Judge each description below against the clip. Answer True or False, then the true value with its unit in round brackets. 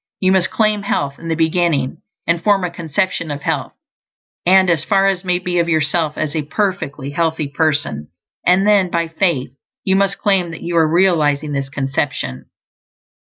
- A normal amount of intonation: True (4.2 semitones)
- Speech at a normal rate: True (175 wpm)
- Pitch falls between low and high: True (165 Hz)